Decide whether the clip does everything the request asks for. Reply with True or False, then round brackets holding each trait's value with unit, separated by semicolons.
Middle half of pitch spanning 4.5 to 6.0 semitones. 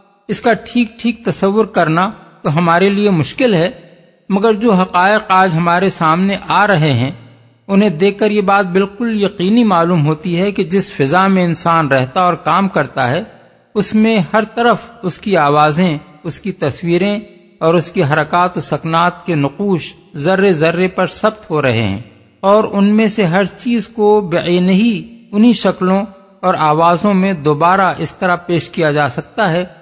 False (3.5 semitones)